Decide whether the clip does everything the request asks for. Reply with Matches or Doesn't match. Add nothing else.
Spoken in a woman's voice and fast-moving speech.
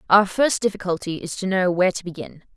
Matches